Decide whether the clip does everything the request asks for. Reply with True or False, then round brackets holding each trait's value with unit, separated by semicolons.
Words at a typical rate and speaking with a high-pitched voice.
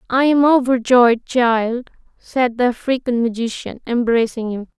False (125 wpm; 240 Hz)